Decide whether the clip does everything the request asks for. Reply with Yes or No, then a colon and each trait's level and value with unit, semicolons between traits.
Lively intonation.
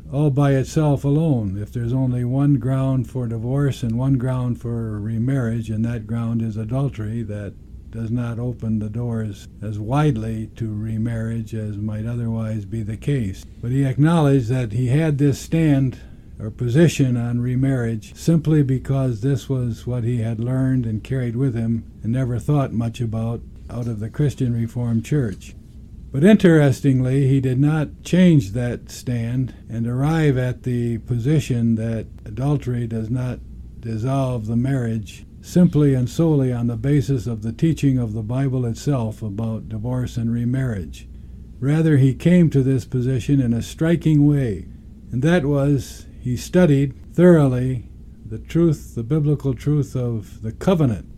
No: average, 3.5 semitones